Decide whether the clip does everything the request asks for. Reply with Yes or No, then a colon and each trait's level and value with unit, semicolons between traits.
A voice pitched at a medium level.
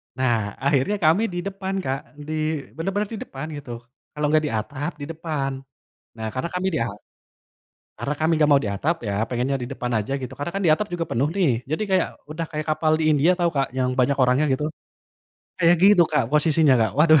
Yes: medium, 150 Hz